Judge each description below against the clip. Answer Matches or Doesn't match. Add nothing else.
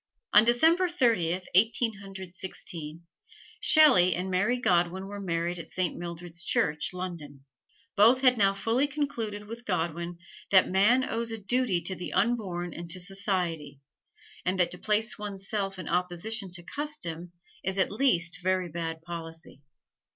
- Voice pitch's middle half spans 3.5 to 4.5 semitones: Matches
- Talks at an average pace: Matches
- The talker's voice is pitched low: Doesn't match